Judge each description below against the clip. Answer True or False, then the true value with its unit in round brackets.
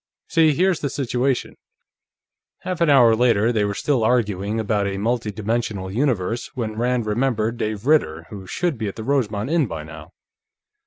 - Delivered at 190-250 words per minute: False (170 wpm)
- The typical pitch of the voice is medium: False (115 Hz)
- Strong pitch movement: False (4.3 semitones)